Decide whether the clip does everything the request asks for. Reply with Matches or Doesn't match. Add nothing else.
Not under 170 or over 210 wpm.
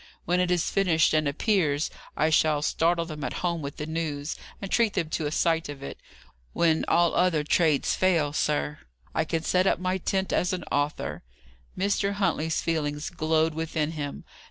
Matches